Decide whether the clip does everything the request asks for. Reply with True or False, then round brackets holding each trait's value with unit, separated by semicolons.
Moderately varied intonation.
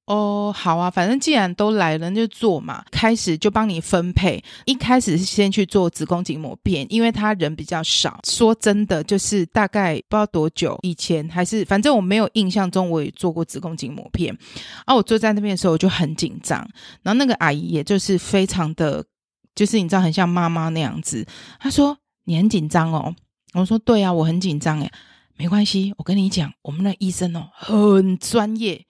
True (4.1 semitones)